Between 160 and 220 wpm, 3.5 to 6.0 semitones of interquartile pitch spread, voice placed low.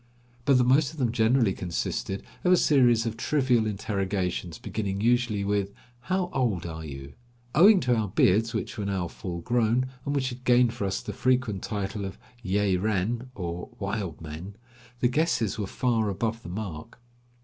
Yes: average, 175 wpm; average, 4.3 semitones; low, 110 Hz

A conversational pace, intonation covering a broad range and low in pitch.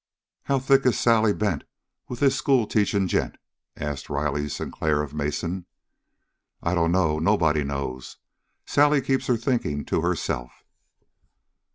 No: slow, 125 wpm; wide, 8.7 semitones; very low, 90 Hz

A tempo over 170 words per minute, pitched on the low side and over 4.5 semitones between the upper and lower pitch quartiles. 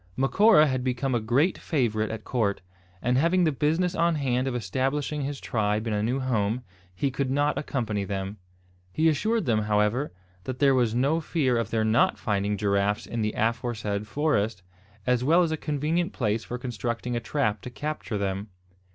Yes: average, 185 wpm; low, 125 Hz; average, 5.2 semitones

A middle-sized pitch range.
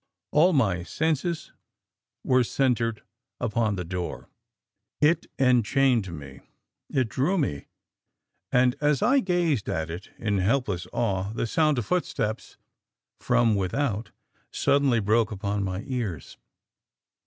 No: wide, 5.8 semitones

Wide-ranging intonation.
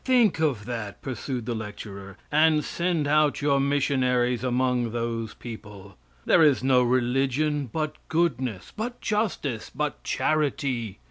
No: average, 4.4 semitones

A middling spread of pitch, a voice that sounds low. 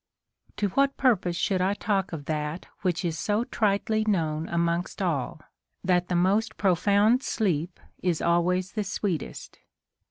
No: average, 3.3 semitones; medium, 185 Hz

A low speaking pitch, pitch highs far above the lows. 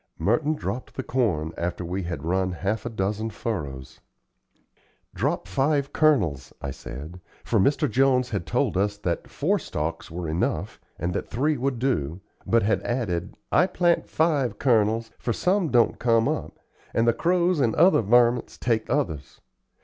Yes: low, 115 Hz; wide, 6.9 semitones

